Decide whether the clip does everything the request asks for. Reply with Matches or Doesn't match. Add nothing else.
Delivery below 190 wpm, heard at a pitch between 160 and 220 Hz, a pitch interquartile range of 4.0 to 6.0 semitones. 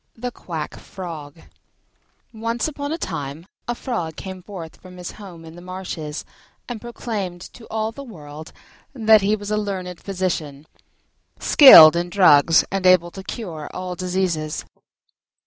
Matches